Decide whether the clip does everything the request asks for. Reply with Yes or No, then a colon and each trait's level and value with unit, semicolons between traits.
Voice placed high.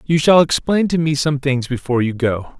No: medium, 145 Hz